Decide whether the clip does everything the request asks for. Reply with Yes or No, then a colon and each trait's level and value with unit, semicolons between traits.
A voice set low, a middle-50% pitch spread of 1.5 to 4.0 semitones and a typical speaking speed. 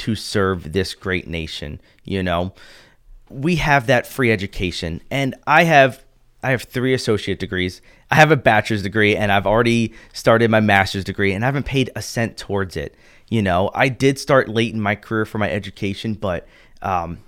No: low, 110 Hz; average, 4.6 semitones; average, 190 wpm